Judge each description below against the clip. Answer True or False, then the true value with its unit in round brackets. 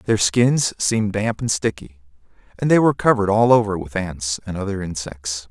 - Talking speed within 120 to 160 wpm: False (185 wpm)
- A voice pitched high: False (100 Hz)